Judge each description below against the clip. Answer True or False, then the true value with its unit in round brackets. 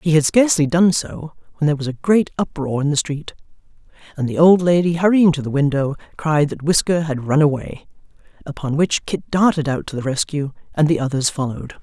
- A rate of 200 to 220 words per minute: True (205 wpm)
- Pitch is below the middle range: False (155 Hz)